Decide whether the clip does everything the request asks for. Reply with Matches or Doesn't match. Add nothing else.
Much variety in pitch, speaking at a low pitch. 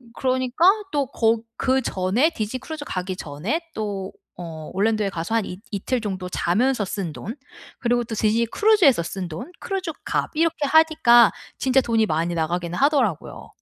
Doesn't match